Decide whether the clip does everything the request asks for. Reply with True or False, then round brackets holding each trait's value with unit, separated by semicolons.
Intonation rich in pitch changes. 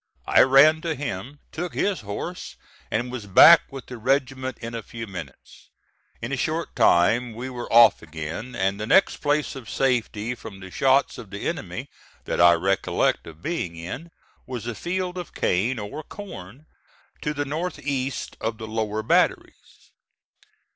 True (5.7 semitones)